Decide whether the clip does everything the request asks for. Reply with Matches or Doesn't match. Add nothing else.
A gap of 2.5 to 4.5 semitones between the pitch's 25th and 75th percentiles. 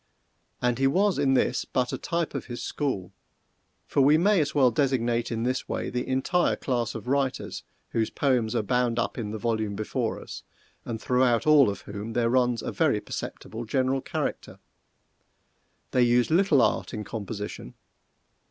Matches